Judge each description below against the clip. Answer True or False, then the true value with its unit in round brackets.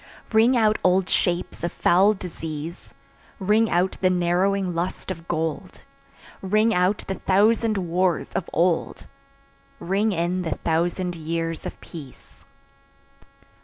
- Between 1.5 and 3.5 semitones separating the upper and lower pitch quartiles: True (2.8 semitones)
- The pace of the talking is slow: True (125 wpm)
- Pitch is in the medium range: True (180 Hz)